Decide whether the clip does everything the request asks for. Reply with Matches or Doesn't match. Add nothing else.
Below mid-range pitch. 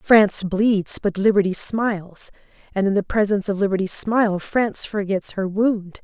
Doesn't match